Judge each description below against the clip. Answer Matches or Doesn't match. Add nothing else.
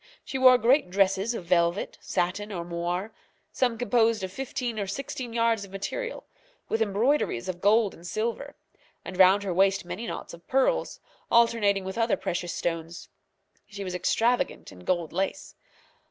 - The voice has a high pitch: Matches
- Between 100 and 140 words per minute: Doesn't match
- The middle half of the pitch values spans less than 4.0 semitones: Doesn't match